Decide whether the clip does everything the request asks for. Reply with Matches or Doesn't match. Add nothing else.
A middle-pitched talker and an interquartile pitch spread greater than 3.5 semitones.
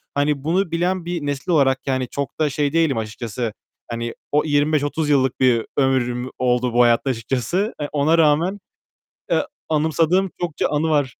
Matches